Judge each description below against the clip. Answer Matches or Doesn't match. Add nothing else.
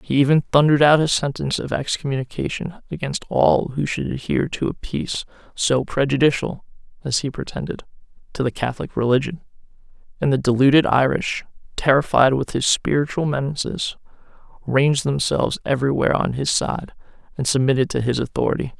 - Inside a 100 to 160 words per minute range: Matches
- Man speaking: Matches